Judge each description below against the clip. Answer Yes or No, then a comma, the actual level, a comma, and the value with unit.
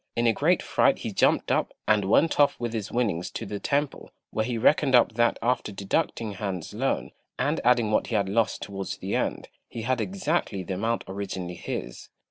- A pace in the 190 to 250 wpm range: Yes, average, 200 wpm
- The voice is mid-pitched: No, low, 115 Hz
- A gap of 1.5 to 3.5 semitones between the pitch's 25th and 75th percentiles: No, average, 4.0 semitones